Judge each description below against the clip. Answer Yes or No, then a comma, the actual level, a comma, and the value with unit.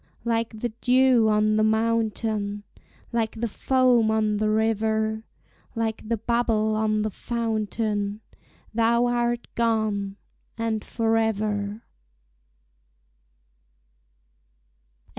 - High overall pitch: Yes, high, 220 Hz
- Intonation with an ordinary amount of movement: No, narrow, 1.3 semitones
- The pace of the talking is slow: Yes, slow, 90 wpm